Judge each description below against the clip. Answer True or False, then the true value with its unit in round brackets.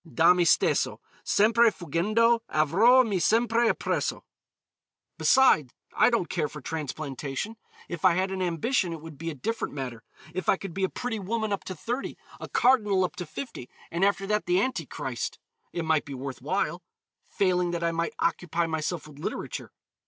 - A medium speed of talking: True (180 wpm)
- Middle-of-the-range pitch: True (180 Hz)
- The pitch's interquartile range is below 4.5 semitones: False (5.3 semitones)